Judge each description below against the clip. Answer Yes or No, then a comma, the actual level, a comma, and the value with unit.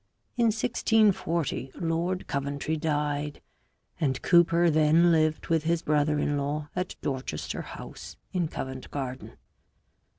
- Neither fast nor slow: No, slow, 120 wpm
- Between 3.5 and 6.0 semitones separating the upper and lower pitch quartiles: No, average, 3.0 semitones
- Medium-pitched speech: Yes, medium, 155 Hz